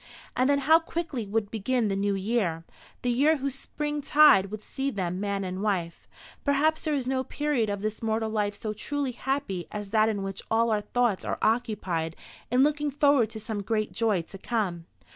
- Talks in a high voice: Yes, high, 220 Hz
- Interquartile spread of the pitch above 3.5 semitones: Yes, average, 5.2 semitones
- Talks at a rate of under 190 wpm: No, average, 200 wpm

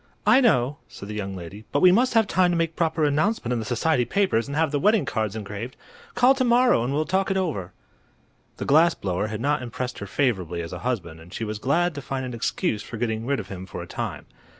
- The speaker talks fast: Yes, fast, 245 wpm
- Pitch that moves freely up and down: Yes, wide, 7.9 semitones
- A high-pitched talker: No, low, 130 Hz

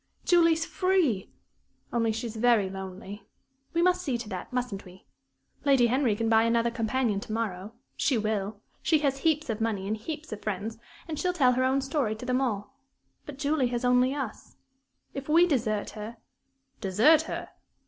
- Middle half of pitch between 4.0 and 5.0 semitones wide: Yes, average, 4.6 semitones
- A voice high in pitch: Yes, high, 240 Hz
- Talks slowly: No, average, 180 wpm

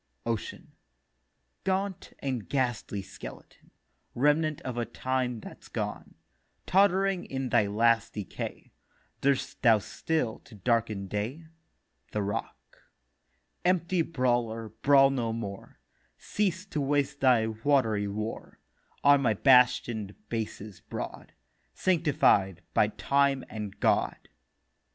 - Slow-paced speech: Yes, slow, 110 wpm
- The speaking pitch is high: No, low, 125 Hz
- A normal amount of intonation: Yes, average, 4.8 semitones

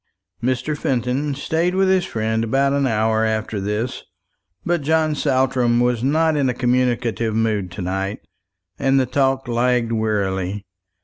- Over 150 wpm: No, average, 145 wpm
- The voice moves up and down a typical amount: Yes, average, 3.8 semitones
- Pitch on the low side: Yes, low, 125 Hz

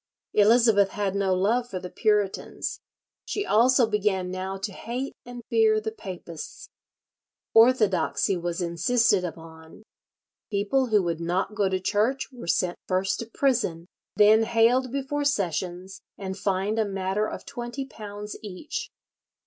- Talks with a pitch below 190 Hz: No, high, 205 Hz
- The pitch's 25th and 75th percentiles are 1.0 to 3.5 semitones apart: No, average, 4.4 semitones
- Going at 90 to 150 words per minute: Yes, average, 140 wpm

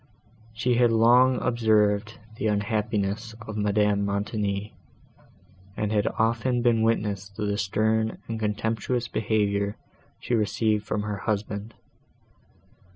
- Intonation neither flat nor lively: No, narrow, 1.8 semitones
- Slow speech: Yes, slow, 115 wpm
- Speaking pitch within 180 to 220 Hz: No, low, 110 Hz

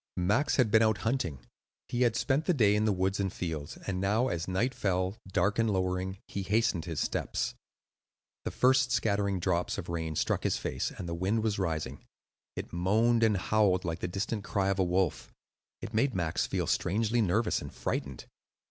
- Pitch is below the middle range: Yes, low, 100 Hz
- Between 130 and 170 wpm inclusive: No, average, 190 wpm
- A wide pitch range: No, average, 3.7 semitones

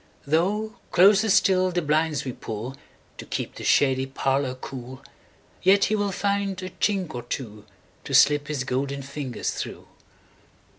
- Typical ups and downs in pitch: No, wide, 6.3 semitones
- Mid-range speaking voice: Yes, medium, 150 Hz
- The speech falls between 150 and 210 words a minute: No, slow, 135 wpm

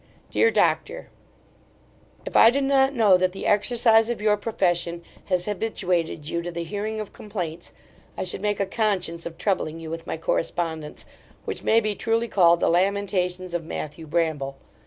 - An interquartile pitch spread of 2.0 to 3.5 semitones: No, average, 4.1 semitones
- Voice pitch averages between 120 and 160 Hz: No, medium, 185 Hz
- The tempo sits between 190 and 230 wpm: No, average, 170 wpm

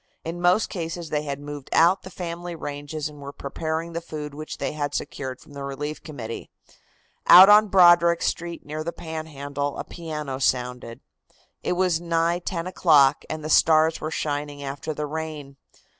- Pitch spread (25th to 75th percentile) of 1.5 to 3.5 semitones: Yes, average, 2.8 semitones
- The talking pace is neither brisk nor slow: Yes, average, 175 wpm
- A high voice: No, medium, 155 Hz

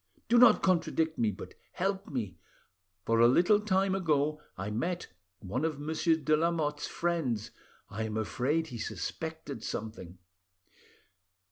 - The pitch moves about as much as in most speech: No, wide, 7.1 semitones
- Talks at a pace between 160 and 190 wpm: No, slow, 135 wpm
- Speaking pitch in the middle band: Yes, medium, 150 Hz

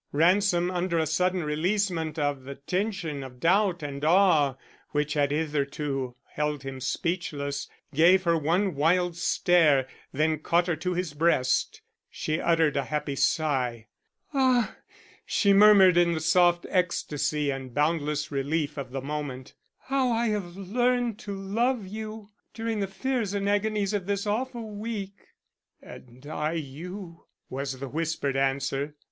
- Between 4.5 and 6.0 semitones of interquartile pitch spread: Yes, wide, 5.4 semitones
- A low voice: No, medium, 165 Hz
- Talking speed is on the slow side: No, average, 145 wpm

